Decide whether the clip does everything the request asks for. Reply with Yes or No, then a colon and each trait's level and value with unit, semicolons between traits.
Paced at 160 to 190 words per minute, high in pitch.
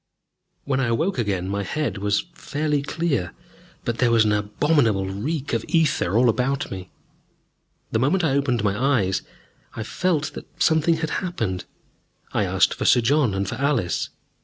No: average, 165 wpm; low, 125 Hz